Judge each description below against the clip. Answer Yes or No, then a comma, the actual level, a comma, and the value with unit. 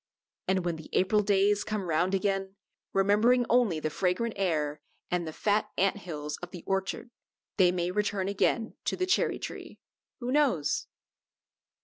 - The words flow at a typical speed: Yes, average, 155 wpm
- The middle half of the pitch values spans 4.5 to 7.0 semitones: No, average, 2.9 semitones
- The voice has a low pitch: No, high, 195 Hz